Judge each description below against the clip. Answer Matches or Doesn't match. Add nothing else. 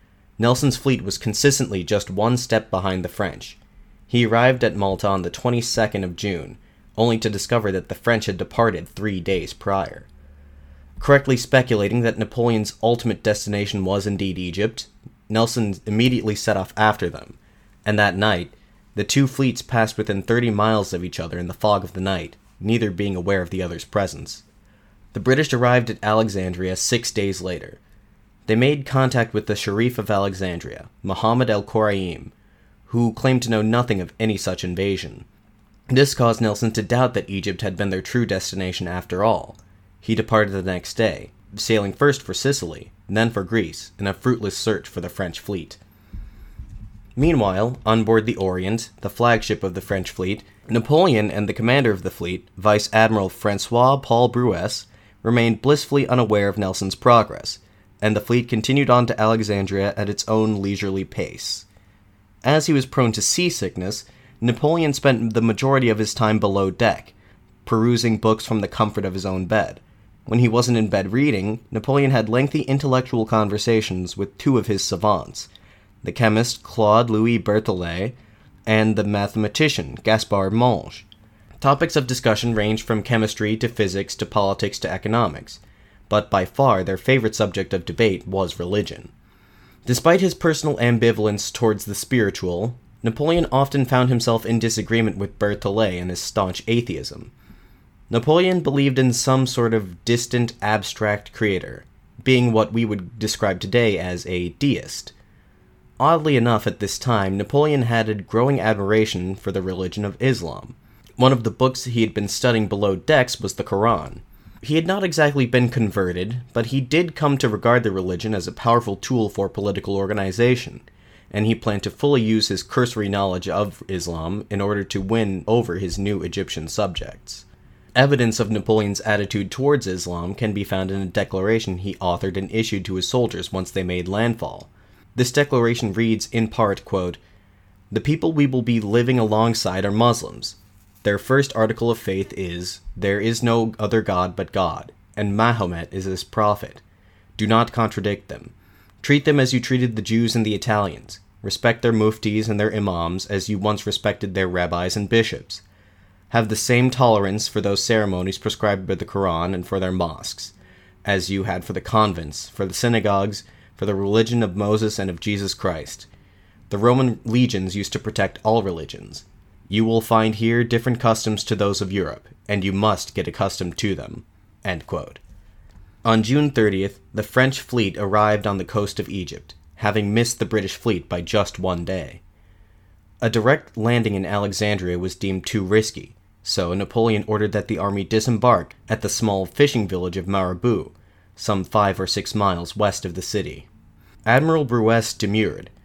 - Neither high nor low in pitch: Doesn't match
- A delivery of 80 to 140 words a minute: Doesn't match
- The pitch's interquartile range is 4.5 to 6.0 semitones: Doesn't match